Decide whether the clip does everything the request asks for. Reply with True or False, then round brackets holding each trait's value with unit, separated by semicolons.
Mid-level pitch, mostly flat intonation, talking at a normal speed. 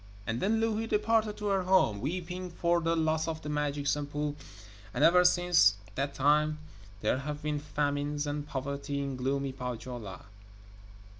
False (150 Hz; 3.7 semitones; 155 wpm)